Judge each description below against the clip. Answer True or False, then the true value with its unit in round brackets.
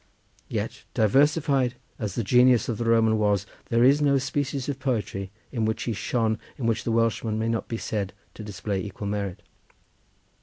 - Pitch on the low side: True (115 Hz)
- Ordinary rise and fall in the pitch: True (3.3 semitones)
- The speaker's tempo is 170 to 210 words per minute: True (180 wpm)